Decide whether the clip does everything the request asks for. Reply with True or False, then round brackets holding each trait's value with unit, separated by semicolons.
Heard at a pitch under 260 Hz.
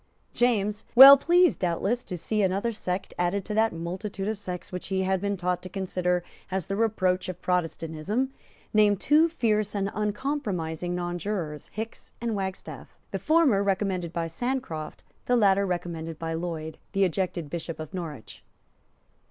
True (190 Hz)